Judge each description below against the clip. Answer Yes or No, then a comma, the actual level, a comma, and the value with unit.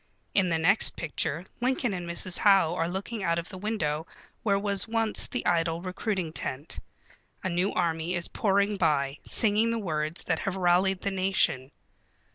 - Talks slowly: No, average, 170 wpm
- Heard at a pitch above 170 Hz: Yes, medium, 185 Hz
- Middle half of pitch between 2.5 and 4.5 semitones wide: Yes, average, 3.4 semitones